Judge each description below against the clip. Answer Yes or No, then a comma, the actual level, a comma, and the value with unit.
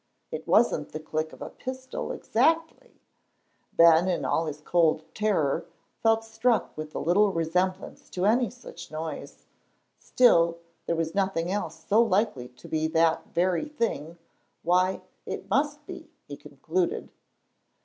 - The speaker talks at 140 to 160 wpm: Yes, average, 145 wpm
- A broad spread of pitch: Yes, wide, 5.8 semitones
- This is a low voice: No, medium, 185 Hz